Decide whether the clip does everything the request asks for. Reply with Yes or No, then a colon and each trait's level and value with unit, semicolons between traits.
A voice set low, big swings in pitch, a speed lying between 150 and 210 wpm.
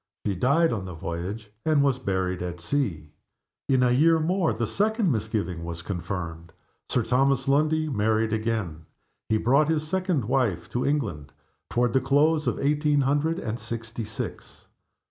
Yes: low, 120 Hz; wide, 6.8 semitones; average, 160 wpm